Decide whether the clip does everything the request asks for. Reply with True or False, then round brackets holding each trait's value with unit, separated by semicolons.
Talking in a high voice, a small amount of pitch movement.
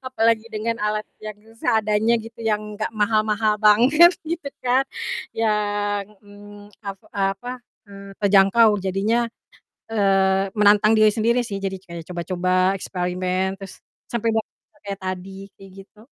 True (210 Hz; 2.3 semitones)